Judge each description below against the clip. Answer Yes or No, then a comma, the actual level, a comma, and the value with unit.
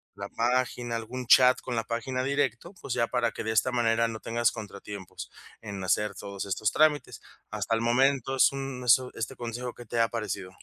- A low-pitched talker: Yes, low, 120 Hz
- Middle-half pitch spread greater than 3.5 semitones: No, narrow, 2.4 semitones